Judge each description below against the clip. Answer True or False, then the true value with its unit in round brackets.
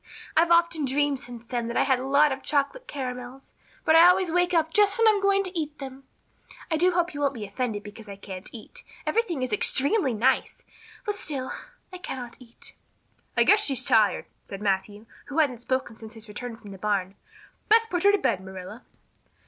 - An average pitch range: False (7.0 semitones)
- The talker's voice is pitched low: False (270 Hz)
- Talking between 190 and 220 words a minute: True (205 wpm)